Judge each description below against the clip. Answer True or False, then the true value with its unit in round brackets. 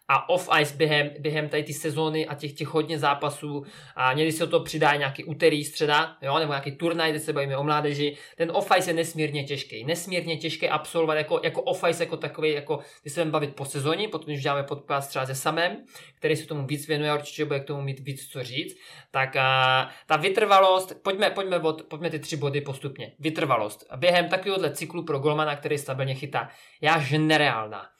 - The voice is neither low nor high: True (155 Hz)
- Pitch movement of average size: False (2.2 semitones)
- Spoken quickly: True (210 wpm)